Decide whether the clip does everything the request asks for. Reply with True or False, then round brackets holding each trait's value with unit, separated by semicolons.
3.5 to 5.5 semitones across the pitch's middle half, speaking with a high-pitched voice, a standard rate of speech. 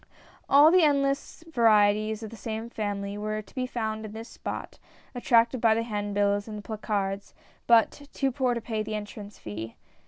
False (2.5 semitones; 220 Hz; 185 wpm)